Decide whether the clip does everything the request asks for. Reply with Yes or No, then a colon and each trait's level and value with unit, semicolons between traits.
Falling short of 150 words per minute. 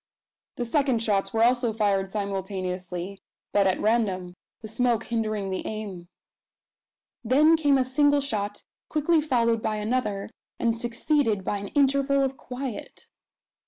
Yes: slow, 135 wpm